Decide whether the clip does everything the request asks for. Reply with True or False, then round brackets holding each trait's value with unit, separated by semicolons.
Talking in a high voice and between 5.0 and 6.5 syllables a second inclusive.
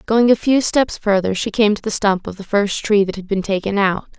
True (205 Hz; 5.3 syllables/s)